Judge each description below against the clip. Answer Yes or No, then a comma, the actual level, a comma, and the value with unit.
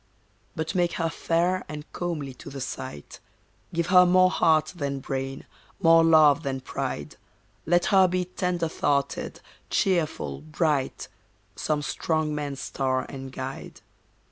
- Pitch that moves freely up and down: No, average, 4.0 semitones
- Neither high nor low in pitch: Yes, medium, 155 Hz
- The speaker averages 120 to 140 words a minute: Yes, slow, 135 wpm